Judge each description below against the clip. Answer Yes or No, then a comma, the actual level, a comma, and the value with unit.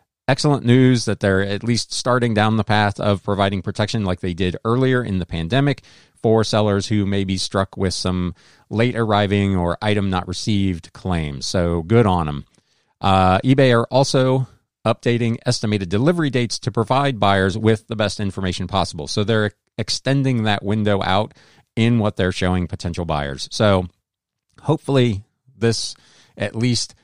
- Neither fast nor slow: Yes, average, 160 wpm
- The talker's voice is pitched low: Yes, low, 105 Hz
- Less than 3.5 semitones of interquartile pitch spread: No, average, 3.8 semitones